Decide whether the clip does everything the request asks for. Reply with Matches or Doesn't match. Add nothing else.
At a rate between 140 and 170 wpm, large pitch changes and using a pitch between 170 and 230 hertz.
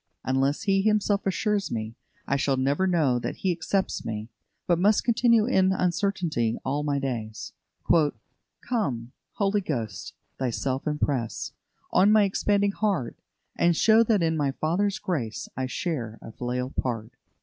Doesn't match